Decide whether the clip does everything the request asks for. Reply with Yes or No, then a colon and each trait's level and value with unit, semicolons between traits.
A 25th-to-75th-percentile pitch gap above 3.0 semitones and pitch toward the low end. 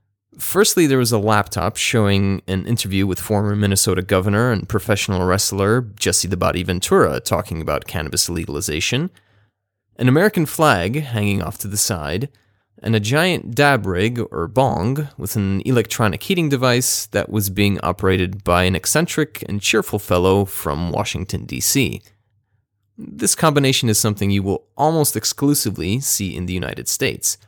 Yes: average, 3.7 semitones; low, 105 Hz